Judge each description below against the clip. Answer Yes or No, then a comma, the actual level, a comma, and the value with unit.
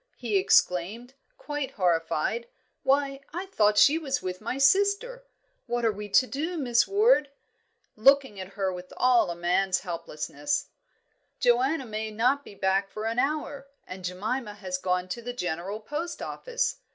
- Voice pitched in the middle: No, high, 235 Hz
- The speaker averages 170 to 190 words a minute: No, average, 155 wpm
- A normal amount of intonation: No, wide, 6.8 semitones